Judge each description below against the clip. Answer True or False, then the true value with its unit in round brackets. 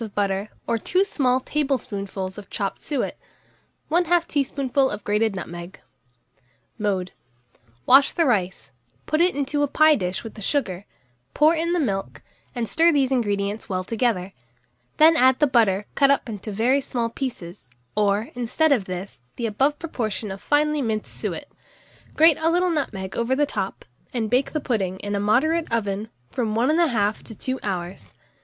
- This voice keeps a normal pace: True (165 wpm)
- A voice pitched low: False (230 Hz)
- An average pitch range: False (6.2 semitones)